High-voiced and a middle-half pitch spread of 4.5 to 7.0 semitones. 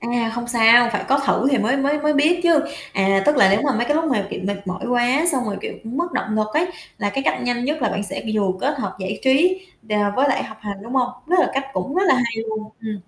Yes: high, 245 Hz; average, 5.0 semitones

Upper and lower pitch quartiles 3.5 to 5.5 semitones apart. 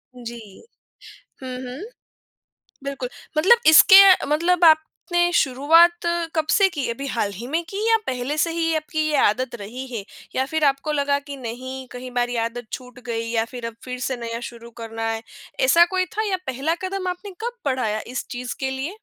Yes: average, 5.2 semitones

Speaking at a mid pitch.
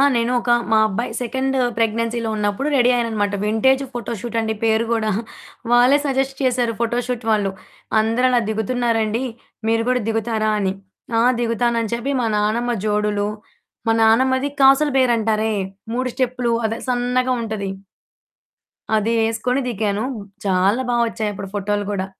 No: high, 230 Hz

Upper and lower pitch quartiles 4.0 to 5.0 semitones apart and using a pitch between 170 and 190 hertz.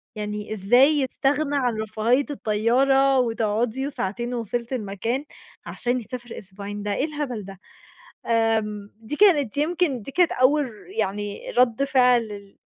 No: average, 4.5 semitones; high, 240 Hz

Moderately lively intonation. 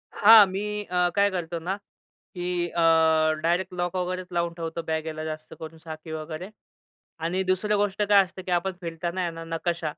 No: narrow, 2.2 semitones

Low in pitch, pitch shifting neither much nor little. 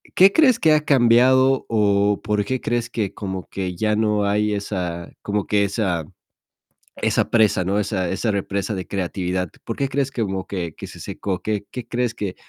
Yes: low, 105 Hz; average, 3.7 semitones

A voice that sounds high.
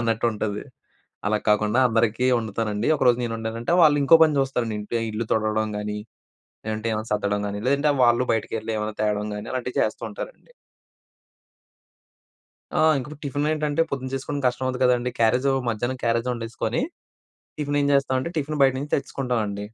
No: low, 120 Hz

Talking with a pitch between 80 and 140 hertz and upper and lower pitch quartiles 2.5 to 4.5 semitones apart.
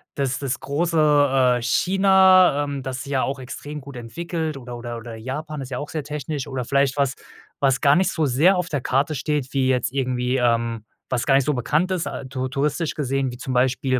Yes: low, 135 Hz; average, 2.9 semitones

